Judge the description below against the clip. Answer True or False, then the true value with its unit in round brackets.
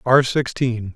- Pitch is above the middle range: False (120 Hz)